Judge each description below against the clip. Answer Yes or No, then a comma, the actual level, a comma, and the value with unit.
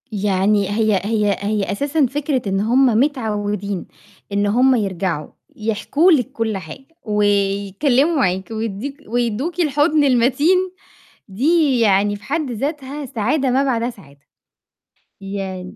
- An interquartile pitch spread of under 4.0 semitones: No, average, 5.2 semitones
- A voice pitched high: Yes, high, 225 Hz